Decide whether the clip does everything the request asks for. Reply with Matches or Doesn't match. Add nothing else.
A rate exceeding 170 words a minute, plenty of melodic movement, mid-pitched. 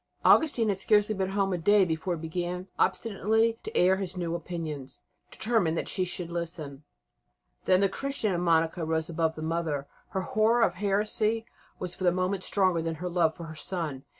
Doesn't match